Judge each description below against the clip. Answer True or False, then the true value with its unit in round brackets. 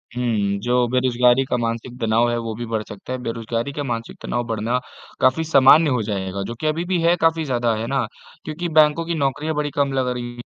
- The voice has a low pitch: True (125 Hz)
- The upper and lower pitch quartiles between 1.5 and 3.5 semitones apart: False (4.2 semitones)